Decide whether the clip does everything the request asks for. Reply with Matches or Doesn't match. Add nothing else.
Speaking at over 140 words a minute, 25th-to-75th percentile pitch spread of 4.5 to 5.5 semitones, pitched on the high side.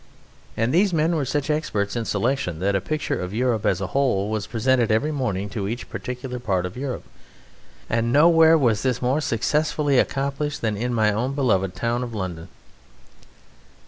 Doesn't match